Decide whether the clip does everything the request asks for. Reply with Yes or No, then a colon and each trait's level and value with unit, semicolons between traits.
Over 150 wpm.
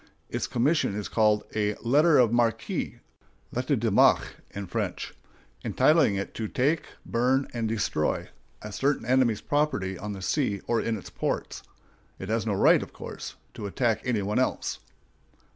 Yes: average, 160 wpm